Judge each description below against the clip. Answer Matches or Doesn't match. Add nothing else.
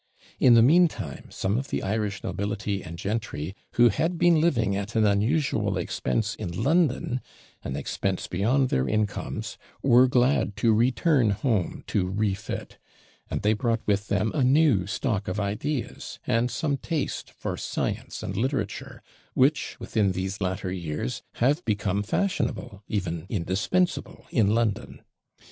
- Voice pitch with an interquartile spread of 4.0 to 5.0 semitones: Matches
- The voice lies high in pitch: Doesn't match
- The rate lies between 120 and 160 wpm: Matches